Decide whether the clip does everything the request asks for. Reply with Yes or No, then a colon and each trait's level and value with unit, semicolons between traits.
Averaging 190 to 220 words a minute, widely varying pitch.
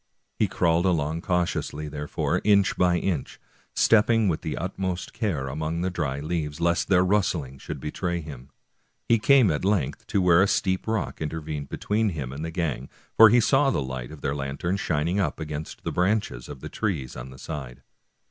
No: average, 195 wpm; average, 4.7 semitones